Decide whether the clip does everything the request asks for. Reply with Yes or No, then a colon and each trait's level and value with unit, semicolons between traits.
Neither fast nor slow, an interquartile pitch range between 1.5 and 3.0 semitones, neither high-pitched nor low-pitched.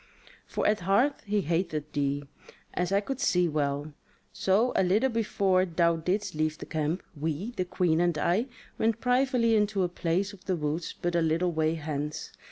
No: average, 180 wpm; average, 4.5 semitones; medium, 180 Hz